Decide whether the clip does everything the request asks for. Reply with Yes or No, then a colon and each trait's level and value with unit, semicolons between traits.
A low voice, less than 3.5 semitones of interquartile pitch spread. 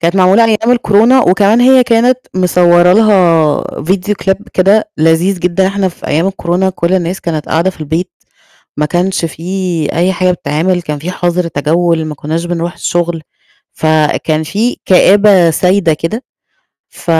No: medium, 180 Hz; average, 2.8 semitones